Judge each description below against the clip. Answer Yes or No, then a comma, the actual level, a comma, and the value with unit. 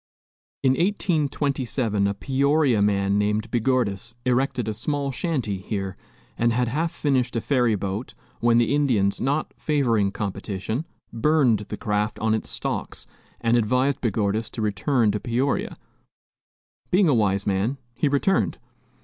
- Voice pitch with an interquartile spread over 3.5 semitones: Yes, average, 4.8 semitones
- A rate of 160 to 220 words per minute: No, average, 140 wpm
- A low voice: Yes, low, 115 Hz